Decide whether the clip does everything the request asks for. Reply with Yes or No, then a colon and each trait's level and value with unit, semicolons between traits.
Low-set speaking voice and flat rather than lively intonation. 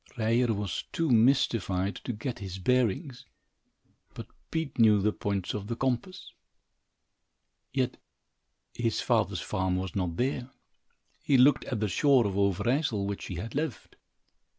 No: low, 115 Hz; average, 4.7 semitones